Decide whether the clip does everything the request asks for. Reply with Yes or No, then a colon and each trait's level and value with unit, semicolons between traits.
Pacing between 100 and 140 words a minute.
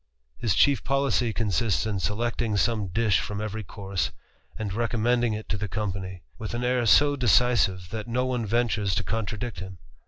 No: average, 175 wpm